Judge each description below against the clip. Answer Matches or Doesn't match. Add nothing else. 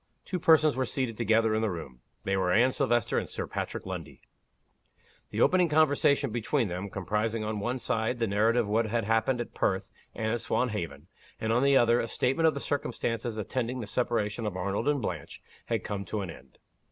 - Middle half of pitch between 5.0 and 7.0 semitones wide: Doesn't match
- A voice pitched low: Matches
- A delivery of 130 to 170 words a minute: Doesn't match